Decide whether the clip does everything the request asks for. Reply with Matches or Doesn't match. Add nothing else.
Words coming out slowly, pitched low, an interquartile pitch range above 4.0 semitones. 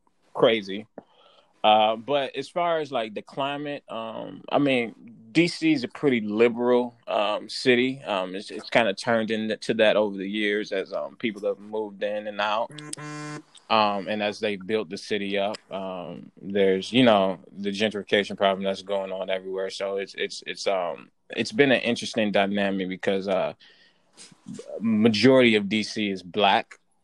Doesn't match